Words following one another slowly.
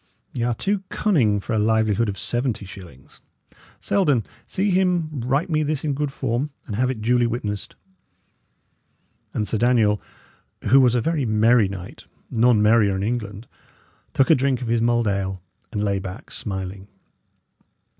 No: average, 160 wpm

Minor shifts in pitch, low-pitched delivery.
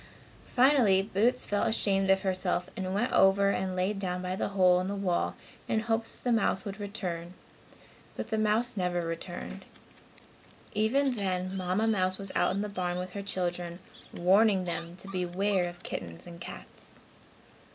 No: narrow, 2.3 semitones; high, 190 Hz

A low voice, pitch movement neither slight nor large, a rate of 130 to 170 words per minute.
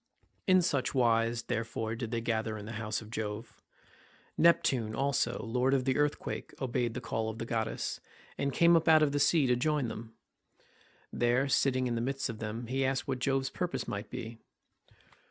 No: low, 120 Hz; average, 3.3 semitones; average, 190 wpm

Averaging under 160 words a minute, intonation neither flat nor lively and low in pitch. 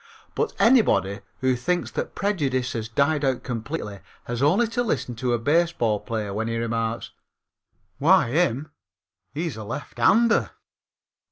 No: average, 140 wpm; wide, 6.6 semitones; low, 130 Hz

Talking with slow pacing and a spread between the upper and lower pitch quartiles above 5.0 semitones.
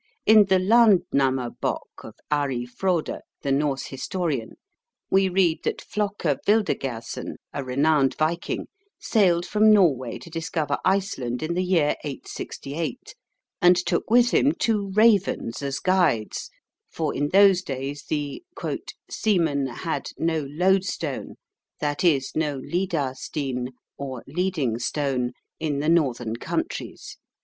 Yes: slow, 120 wpm; wide, 5.5 semitones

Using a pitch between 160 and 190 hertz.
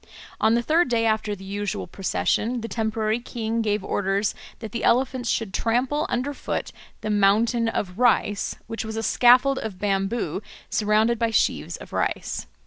No: high, 225 Hz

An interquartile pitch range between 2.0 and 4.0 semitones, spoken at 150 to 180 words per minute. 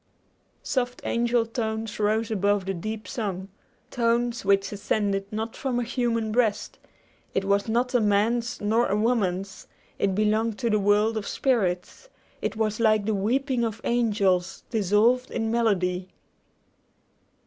No: average, 2.7 semitones; average, 140 wpm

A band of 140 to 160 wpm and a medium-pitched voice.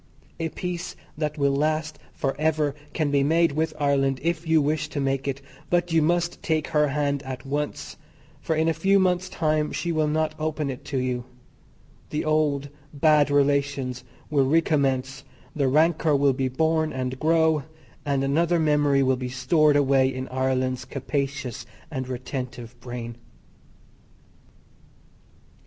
Yes: average, 155 wpm; medium, 145 Hz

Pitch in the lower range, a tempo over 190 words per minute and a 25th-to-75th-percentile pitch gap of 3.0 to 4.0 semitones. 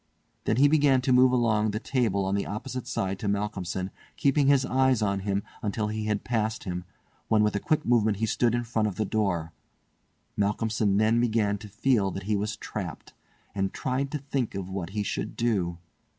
Yes: low, 110 Hz; average, 200 wpm; average, 3.4 semitones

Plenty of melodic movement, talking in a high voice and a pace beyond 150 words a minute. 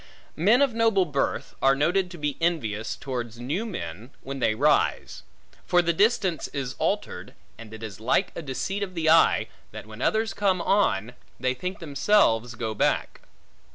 No: wide, 8.0 semitones; medium, 150 Hz; average, 170 wpm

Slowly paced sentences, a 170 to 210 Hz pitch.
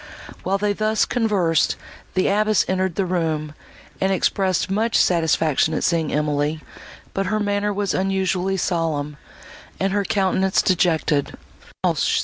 Yes: slow, 130 wpm; medium, 185 Hz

